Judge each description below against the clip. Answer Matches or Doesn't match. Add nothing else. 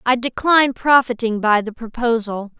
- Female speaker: Matches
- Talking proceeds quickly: Doesn't match